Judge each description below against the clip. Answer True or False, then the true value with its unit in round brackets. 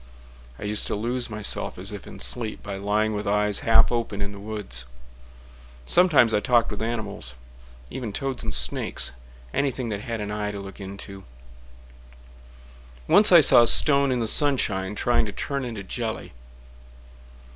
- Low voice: True (105 Hz)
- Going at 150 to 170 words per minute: True (160 wpm)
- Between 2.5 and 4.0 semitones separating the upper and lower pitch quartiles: True (3.2 semitones)